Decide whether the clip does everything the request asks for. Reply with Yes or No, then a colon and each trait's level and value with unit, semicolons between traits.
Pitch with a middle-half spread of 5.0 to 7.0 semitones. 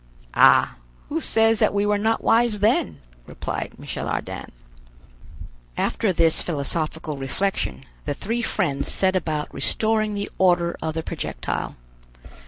Yes: wide, 5.4 semitones